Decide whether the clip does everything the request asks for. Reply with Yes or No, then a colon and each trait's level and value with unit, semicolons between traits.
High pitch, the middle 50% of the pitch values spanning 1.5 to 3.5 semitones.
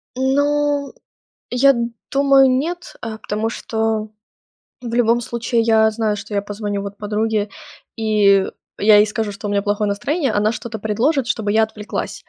Yes: high, 220 Hz; average, 3.0 semitones